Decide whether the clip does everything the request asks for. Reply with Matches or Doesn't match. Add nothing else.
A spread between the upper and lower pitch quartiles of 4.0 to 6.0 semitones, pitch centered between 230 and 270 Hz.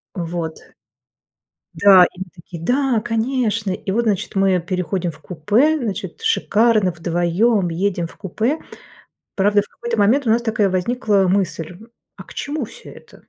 Doesn't match